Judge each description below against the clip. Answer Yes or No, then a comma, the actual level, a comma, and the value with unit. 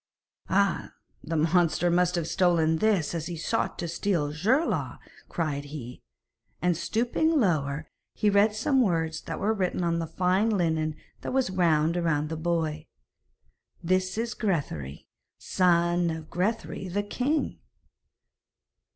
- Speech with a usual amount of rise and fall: Yes, average, 3.9 semitones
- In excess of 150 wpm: No, slow, 135 wpm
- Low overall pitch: No, medium, 175 Hz